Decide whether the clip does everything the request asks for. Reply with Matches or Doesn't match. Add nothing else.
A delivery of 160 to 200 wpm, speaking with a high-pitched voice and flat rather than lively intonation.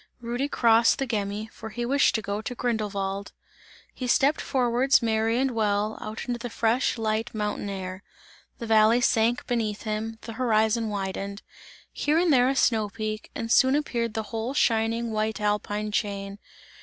Matches